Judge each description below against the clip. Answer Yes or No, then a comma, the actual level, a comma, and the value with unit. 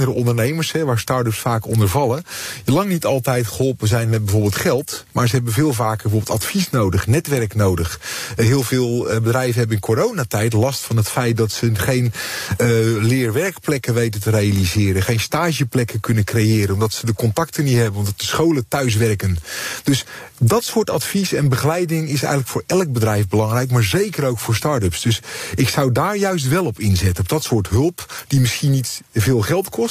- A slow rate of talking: No, average, 185 wpm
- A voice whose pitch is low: Yes, low, 120 Hz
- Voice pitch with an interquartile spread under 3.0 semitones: No, average, 4.3 semitones